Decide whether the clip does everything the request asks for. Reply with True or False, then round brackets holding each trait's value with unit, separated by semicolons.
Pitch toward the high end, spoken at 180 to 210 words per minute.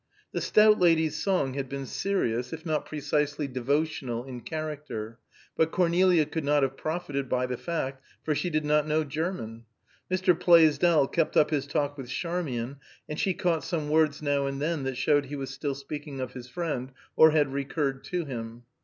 False (150 Hz; 185 wpm)